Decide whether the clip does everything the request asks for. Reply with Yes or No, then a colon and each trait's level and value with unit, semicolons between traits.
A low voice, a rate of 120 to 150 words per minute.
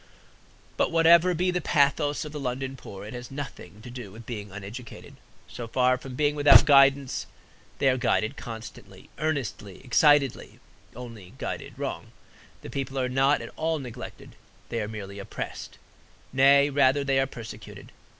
No: low, 130 Hz; average, 160 wpm